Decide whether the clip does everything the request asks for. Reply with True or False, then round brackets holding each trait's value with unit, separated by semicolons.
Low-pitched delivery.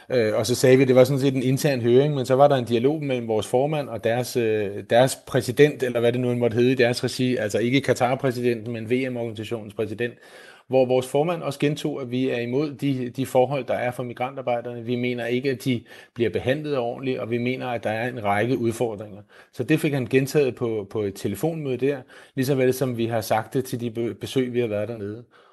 True (125 Hz)